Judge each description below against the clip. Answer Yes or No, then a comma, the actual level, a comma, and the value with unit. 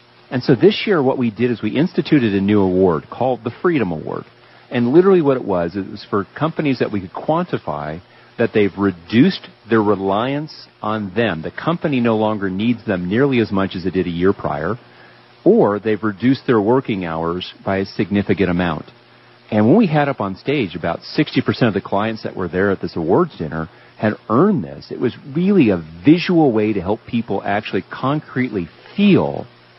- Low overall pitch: Yes, low, 110 Hz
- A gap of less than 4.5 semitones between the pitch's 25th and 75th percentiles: No, average, 5.2 semitones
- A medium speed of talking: Yes, average, 195 wpm